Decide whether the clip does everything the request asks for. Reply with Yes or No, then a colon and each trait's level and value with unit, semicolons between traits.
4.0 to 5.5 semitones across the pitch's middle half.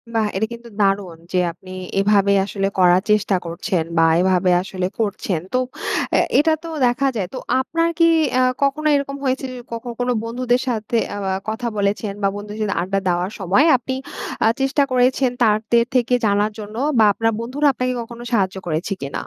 Yes: average, 4.4 semitones